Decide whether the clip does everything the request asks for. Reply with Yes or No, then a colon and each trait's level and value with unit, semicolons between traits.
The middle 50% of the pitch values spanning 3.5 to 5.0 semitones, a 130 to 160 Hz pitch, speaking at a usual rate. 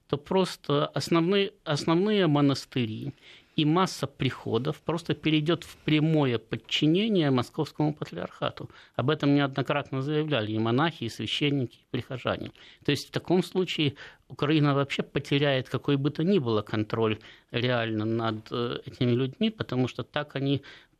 Yes: average, 4.1 semitones; medium, 140 Hz; average, 135 wpm